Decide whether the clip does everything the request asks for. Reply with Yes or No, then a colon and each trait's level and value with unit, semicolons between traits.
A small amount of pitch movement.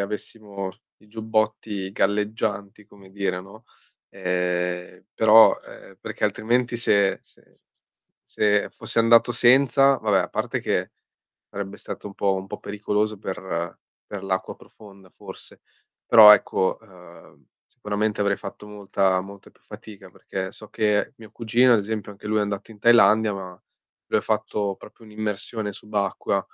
Yes: narrow, 2.0 semitones